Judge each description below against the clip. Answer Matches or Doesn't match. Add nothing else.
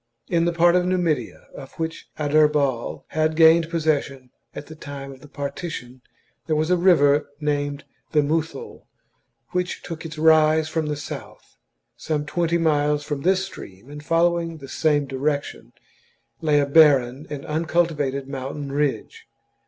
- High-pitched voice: Doesn't match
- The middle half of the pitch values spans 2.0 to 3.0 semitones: Matches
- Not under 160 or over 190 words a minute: Doesn't match